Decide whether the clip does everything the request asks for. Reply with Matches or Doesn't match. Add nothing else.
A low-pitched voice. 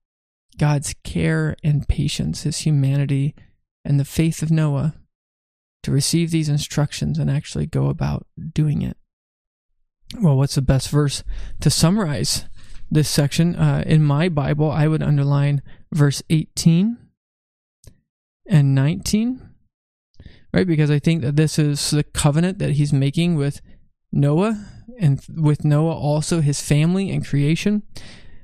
Doesn't match